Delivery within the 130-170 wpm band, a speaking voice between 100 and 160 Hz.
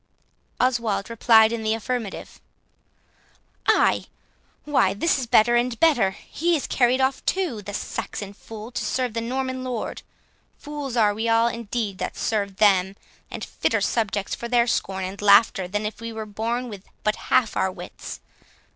No: average, 165 wpm; high, 230 Hz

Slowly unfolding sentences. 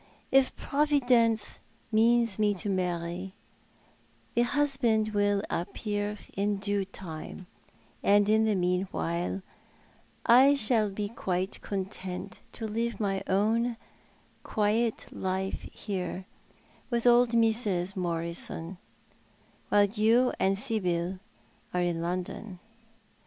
Yes: slow, 105 wpm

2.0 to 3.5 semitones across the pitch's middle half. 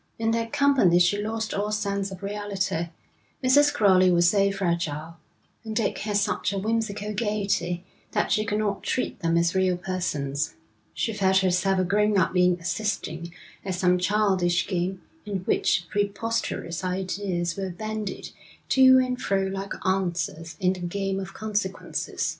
Yes: average, 2.8 semitones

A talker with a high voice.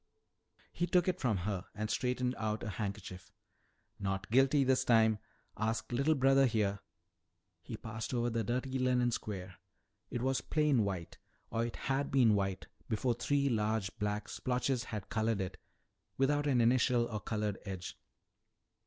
No: low, 115 Hz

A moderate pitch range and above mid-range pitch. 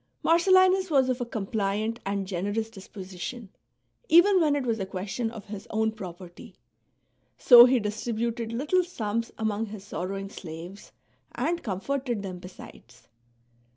Yes: average, 4.4 semitones; high, 220 Hz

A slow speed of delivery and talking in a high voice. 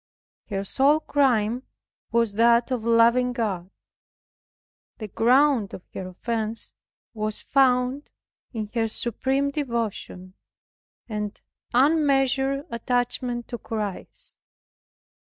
Yes: slow, 95 wpm; high, 235 Hz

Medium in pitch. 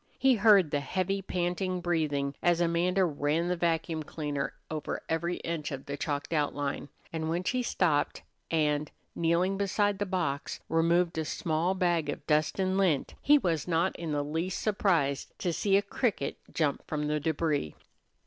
Yes: medium, 165 Hz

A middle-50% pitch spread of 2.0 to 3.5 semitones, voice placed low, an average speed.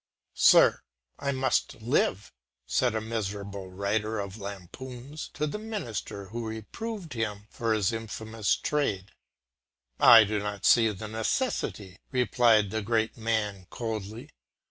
No: average, 2.8 semitones; low, 110 Hz; slow, 125 wpm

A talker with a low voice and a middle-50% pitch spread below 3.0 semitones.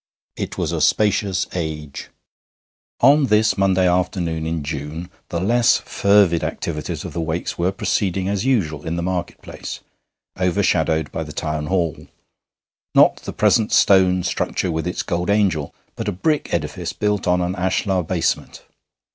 No: very low, 90 Hz; average, 3.5 semitones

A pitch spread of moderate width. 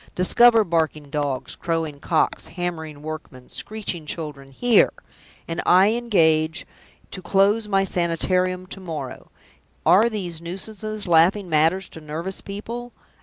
Yes: average, 4.0 semitones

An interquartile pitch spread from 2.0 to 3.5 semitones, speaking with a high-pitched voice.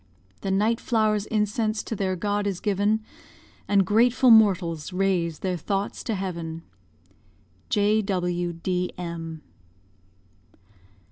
Yes: average, 3.1 semitones; high, 195 Hz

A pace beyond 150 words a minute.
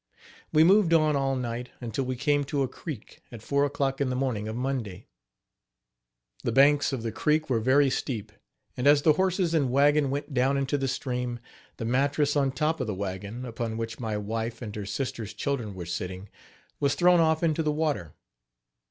Yes: average, 195 wpm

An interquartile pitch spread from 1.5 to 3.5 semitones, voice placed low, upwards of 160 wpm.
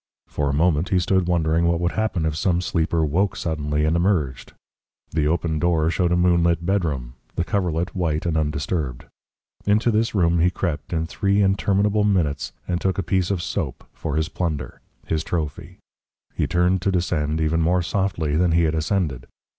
Yes: average, 2.8 semitones; very low, 85 Hz; average, 180 wpm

